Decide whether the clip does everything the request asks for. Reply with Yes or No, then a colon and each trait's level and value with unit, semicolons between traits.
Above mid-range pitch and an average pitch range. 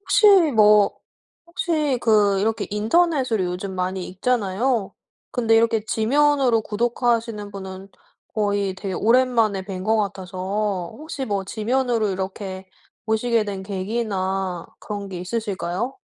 Yes: high, 210 Hz; average, 3.5 semitones